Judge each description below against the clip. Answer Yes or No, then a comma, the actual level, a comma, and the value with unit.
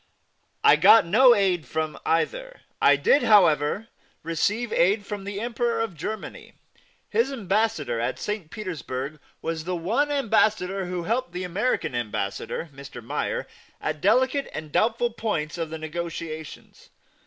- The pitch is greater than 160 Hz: Yes, medium, 185 Hz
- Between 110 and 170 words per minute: Yes, average, 140 wpm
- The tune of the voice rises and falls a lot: Yes, wide, 6.2 semitones